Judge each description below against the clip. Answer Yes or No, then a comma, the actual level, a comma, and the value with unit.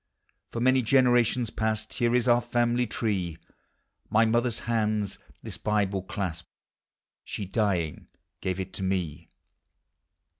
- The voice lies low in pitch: Yes, low, 110 Hz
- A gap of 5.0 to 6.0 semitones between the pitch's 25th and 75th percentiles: No, average, 3.8 semitones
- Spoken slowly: Yes, slow, 115 wpm